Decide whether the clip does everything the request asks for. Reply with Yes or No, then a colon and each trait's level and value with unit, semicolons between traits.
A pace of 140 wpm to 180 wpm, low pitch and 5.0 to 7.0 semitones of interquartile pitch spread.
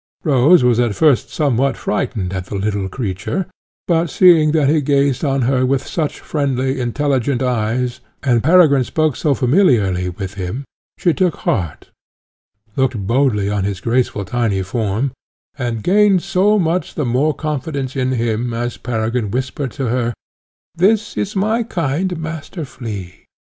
Yes: average, 150 wpm; low, 130 Hz; average, 5.3 semitones